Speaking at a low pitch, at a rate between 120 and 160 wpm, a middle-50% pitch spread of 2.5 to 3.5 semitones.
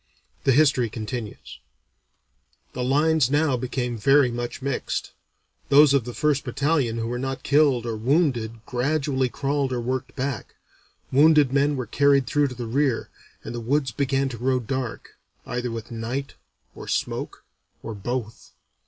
Yes: low, 130 Hz; average, 155 wpm; average, 2.8 semitones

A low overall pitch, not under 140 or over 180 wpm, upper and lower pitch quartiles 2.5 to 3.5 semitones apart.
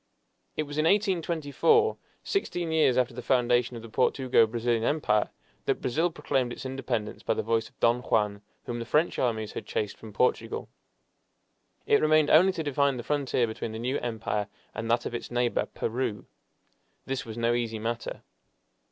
No: low, 120 Hz; average, 175 wpm; average, 4.2 semitones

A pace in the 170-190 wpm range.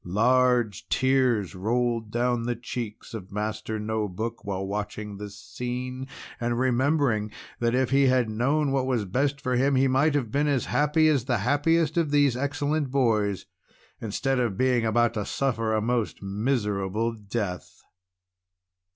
No: average, 155 wpm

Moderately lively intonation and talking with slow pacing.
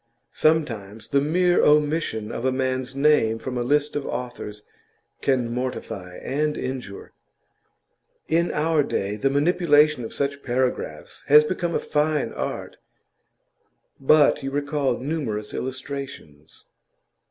Yes: average, 3.7 semitones; slow, 120 wpm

